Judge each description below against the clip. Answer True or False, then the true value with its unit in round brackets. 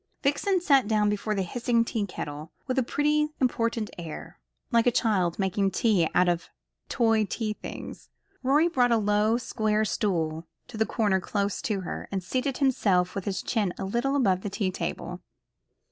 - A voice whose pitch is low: False (215 Hz)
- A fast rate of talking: False (175 wpm)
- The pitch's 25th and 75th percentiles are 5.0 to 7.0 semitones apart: False (4.2 semitones)